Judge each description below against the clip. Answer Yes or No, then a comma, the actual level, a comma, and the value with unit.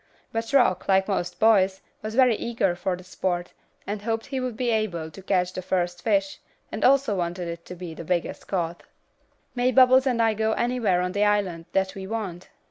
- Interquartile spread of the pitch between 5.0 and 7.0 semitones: No, average, 4.1 semitones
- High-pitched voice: Yes, high, 195 Hz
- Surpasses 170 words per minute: Yes, fast, 205 wpm